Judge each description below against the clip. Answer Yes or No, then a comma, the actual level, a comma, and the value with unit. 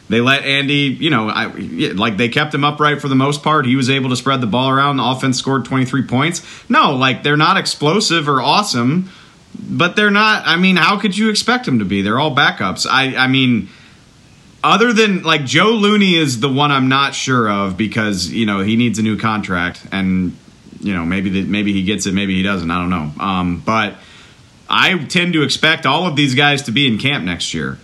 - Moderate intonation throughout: No, wide, 6.1 semitones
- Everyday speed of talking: No, fast, 225 wpm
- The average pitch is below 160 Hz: Yes, low, 135 Hz